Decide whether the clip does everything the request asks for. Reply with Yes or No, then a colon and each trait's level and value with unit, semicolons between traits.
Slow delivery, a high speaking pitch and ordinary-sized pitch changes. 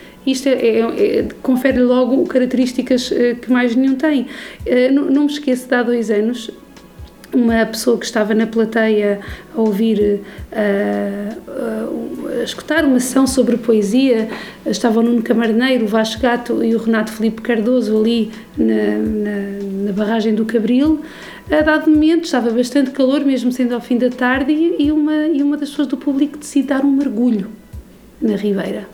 No: average, 175 wpm; high, 245 Hz; average, 3.5 semitones